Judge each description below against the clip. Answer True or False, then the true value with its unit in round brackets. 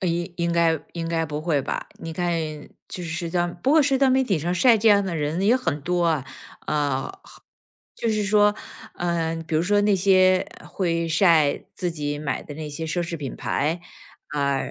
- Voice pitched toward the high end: False (170 Hz)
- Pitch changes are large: False (3.6 semitones)